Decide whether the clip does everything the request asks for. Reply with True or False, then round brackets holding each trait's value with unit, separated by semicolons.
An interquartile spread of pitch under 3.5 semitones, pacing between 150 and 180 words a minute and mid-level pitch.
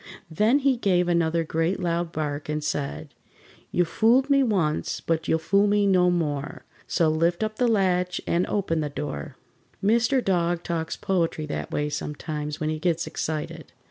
False (4.1 semitones; 170 wpm; 170 Hz)